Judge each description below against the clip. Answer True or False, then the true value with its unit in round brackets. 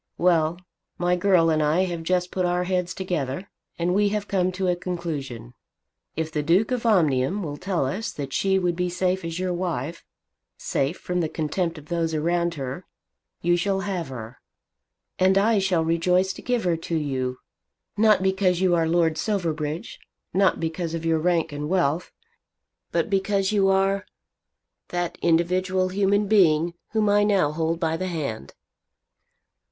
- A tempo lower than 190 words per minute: True (170 wpm)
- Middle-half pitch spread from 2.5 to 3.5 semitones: True (2.8 semitones)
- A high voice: False (175 Hz)